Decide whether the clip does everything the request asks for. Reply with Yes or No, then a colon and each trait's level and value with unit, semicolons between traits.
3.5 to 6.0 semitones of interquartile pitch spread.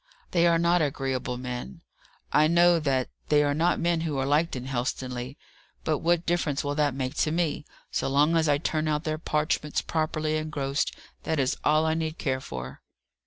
No: average, 3.0 semitones